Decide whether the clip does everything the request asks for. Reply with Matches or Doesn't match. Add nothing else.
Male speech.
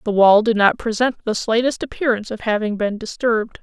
Doesn't match